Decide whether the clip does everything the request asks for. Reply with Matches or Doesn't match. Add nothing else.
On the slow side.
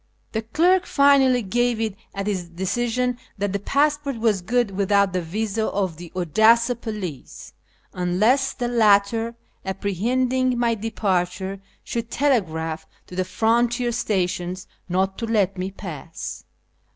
Matches